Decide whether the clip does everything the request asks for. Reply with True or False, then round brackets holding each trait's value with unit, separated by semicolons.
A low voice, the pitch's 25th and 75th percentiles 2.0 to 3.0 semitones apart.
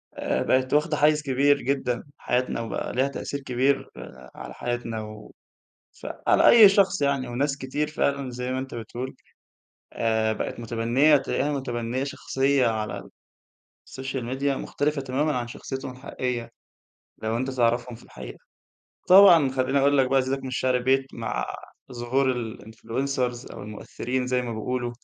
True (130 Hz; 2.5 semitones)